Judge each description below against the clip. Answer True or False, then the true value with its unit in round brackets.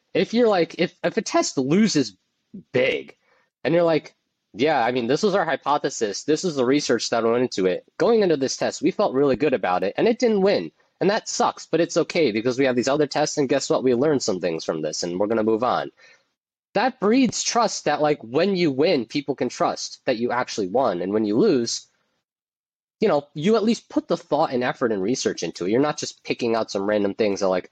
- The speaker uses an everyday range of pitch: False (8.0 semitones)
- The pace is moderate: False (240 wpm)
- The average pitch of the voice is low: False (150 Hz)